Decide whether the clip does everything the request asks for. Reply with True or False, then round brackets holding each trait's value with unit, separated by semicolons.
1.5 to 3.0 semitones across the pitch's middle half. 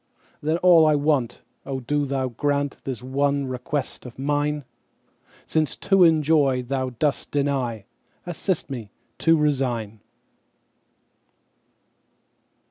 True (2.7 semitones)